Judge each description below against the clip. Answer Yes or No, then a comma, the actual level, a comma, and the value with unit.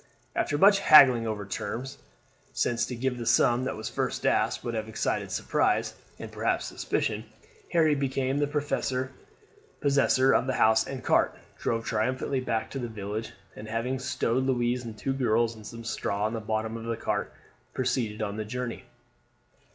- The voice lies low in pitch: Yes, low, 120 Hz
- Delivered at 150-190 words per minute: Yes, average, 175 wpm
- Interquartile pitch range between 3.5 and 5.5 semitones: No, average, 3.0 semitones